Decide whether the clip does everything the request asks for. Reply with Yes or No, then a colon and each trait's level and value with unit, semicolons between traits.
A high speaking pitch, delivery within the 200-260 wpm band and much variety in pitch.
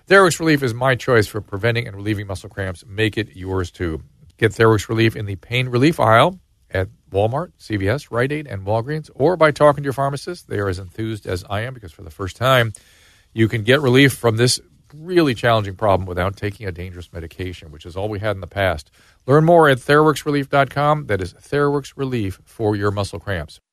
No: low, 110 Hz; fast, 205 wpm; wide, 5.9 semitones